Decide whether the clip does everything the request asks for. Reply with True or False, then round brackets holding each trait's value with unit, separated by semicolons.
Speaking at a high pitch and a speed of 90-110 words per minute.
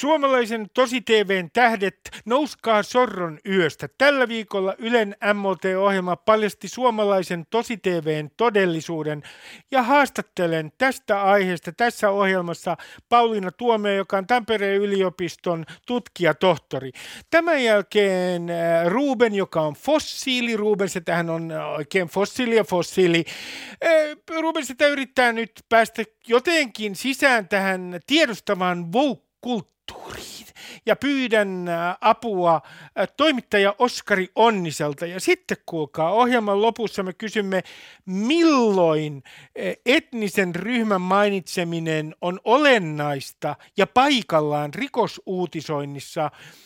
True (200 Hz; 100 wpm)